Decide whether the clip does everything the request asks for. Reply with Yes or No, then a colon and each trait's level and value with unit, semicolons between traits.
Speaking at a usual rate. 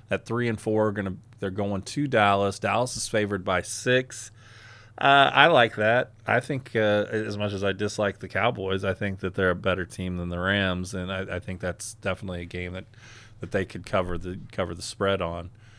No: fast, 215 wpm